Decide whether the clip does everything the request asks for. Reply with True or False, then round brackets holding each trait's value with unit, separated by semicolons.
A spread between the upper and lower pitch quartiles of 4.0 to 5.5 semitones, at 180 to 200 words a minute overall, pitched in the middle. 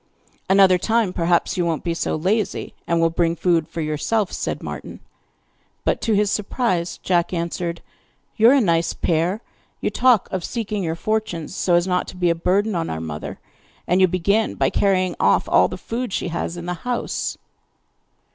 False (3.6 semitones; 185 wpm; 180 Hz)